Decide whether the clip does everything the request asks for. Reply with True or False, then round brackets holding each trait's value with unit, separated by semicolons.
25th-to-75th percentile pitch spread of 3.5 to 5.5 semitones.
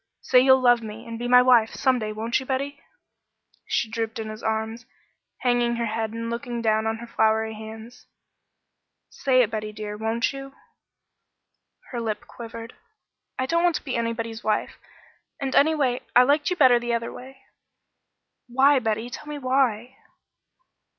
False (2.7 semitones)